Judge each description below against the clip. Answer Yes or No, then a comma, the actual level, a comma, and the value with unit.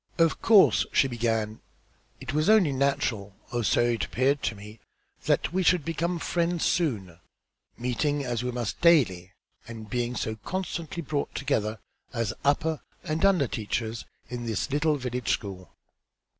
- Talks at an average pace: Yes, average, 150 wpm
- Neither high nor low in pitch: No, low, 125 Hz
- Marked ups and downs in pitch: Yes, wide, 5.8 semitones